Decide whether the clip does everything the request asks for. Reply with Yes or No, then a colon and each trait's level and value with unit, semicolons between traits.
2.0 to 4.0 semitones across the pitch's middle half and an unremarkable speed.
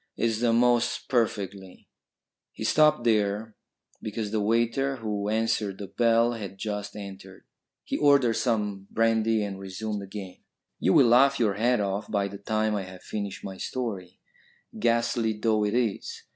Yes: narrow, 2.6 semitones; average, 160 wpm